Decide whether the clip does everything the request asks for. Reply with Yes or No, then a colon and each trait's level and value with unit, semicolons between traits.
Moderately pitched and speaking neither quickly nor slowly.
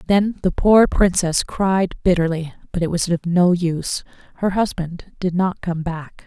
Yes: medium, 180 Hz; average, 170 wpm